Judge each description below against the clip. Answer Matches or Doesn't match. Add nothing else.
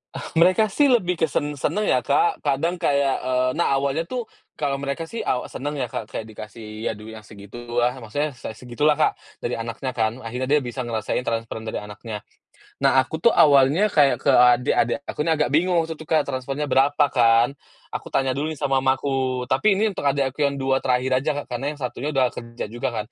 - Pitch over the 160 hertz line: Doesn't match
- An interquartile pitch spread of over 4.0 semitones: Doesn't match